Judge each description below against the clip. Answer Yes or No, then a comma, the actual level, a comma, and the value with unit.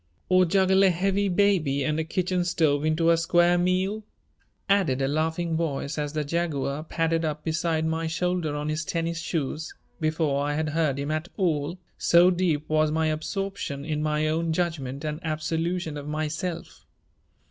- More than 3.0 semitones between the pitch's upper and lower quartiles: No, narrow, 2.4 semitones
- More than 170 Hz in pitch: No, medium, 160 Hz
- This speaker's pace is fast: No, average, 170 wpm